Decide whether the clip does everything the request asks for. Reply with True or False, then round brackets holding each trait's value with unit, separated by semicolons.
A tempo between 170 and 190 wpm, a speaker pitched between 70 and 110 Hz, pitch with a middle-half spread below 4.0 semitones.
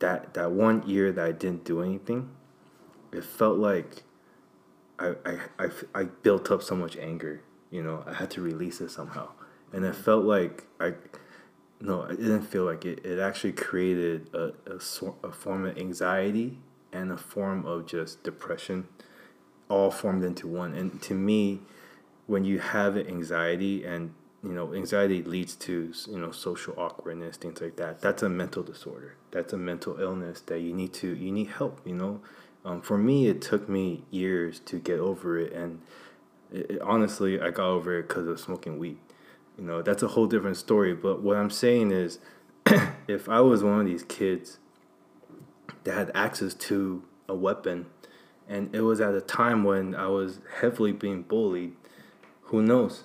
True (180 wpm; 95 Hz; 2.6 semitones)